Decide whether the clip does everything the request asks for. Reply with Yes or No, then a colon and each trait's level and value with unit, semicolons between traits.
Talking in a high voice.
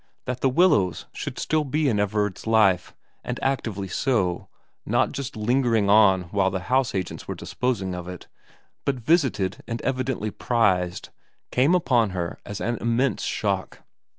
No: low, 110 Hz